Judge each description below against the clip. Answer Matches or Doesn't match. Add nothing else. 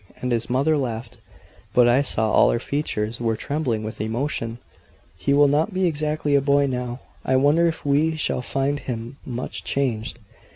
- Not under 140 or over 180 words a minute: Matches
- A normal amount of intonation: Matches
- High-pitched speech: Doesn't match